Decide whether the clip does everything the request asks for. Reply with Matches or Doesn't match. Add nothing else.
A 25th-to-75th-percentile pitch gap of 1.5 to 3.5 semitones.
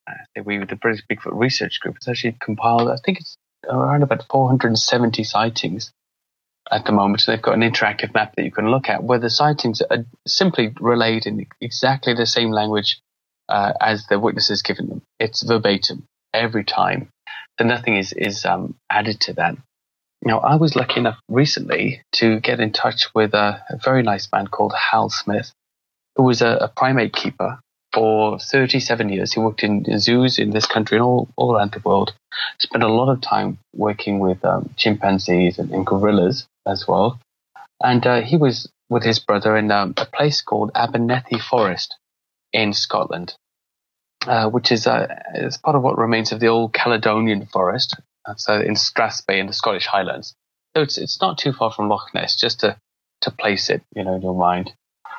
Matches